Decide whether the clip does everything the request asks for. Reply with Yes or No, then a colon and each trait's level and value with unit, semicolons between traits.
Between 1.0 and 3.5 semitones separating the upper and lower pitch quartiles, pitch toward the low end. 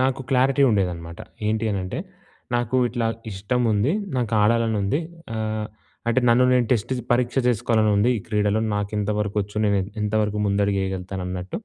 Yes: average, 3.1 semitones; low, 105 Hz